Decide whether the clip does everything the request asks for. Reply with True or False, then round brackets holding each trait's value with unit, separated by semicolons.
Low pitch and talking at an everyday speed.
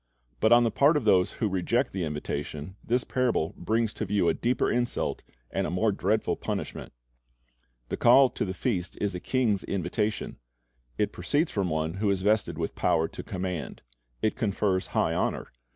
True (105 Hz; 180 wpm)